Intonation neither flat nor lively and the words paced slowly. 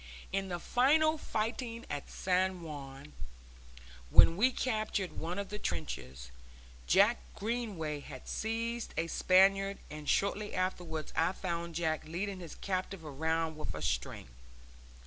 Yes: average, 4.7 semitones; slow, 130 wpm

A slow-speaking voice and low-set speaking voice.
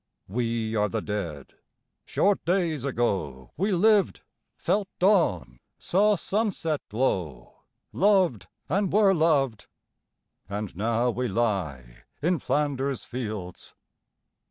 Yes: slow, 105 wpm; low, 125 Hz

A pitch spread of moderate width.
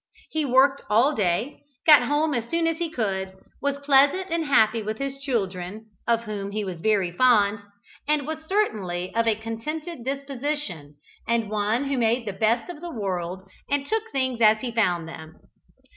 No: wide, 5.7 semitones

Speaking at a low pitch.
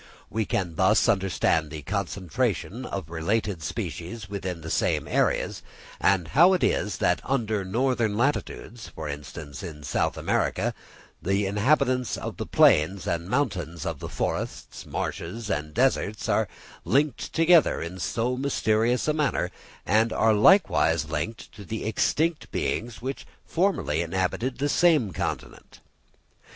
Yes: low, 105 Hz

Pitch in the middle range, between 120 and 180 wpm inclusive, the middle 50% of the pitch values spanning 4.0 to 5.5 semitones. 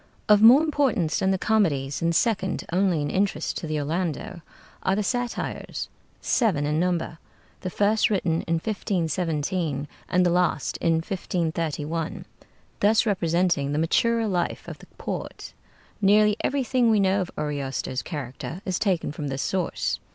Yes: medium, 180 Hz; average, 150 wpm; average, 4.5 semitones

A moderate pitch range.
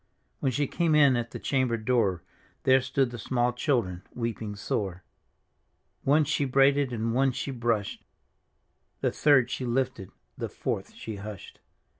Yes: average, 3.3 semitones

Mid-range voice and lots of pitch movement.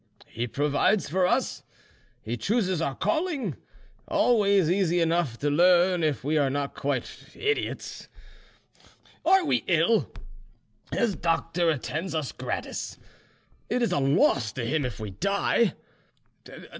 Yes: medium, 165 Hz; wide, 5.8 semitones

